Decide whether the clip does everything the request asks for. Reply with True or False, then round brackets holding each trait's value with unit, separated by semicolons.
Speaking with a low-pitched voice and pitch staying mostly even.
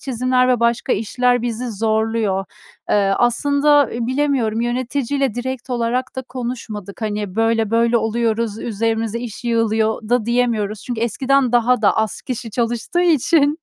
False (235 Hz; 2.3 semitones)